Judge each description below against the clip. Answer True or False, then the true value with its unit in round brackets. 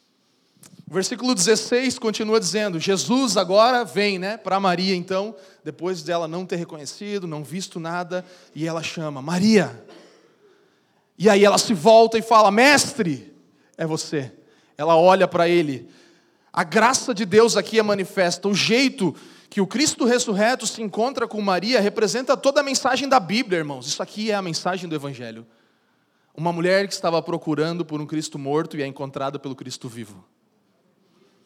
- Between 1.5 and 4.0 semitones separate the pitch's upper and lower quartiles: False (5.3 semitones)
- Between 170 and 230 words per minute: False (160 wpm)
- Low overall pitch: False (190 Hz)